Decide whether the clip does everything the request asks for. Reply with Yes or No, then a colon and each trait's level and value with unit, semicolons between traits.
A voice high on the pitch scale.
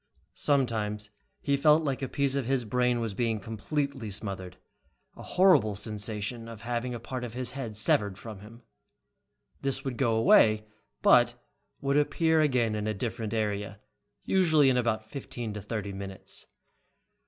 No: low, 115 Hz